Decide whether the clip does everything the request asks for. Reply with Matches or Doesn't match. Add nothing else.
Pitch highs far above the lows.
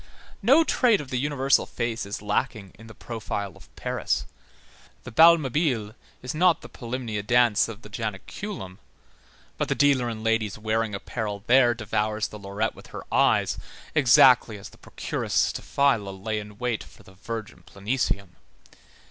Doesn't match